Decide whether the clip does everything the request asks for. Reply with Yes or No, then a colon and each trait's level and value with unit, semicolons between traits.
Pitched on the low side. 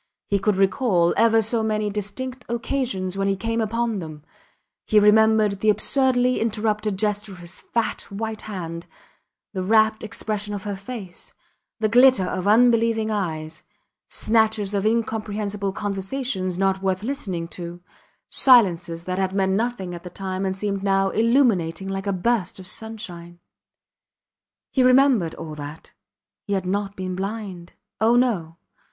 No: high, 205 Hz